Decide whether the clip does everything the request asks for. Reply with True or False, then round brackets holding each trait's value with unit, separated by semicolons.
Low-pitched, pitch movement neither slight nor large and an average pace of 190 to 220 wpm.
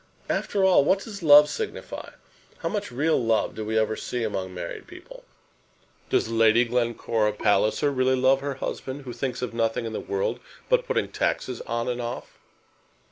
False (125 Hz; 4.3 semitones; 175 wpm)